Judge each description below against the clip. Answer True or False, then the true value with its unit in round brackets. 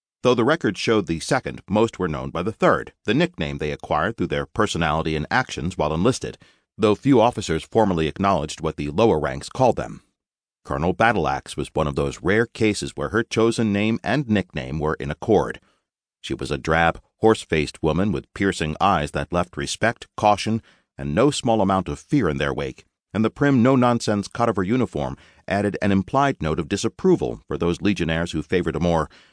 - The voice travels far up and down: True (6.1 semitones)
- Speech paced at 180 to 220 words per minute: True (195 wpm)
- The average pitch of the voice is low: True (95 Hz)